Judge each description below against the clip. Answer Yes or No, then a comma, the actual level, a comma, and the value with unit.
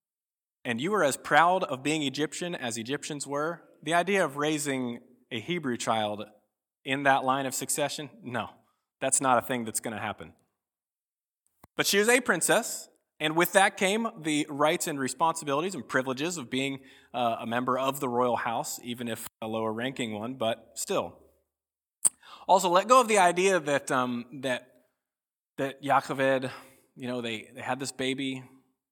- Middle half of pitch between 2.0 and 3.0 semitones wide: No, average, 4.0 semitones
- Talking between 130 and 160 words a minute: No, average, 170 wpm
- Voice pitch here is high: No, low, 135 Hz